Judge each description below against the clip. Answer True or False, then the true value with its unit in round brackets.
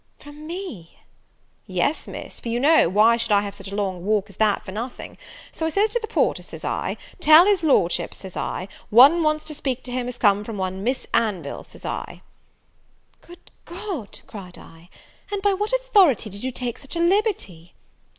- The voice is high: True (245 Hz)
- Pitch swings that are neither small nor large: False (8.9 semitones)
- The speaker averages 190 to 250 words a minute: True (200 wpm)